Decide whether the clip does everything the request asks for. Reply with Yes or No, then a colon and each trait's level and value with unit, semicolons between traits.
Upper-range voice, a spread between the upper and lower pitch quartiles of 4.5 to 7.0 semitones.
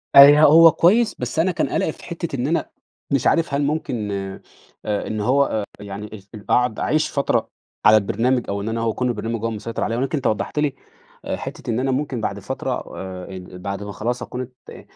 No: low, 120 Hz; average, 5.3 semitones